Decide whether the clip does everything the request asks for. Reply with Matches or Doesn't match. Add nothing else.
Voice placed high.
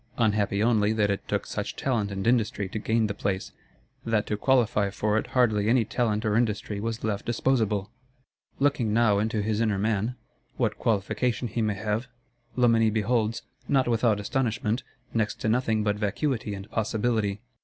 Doesn't match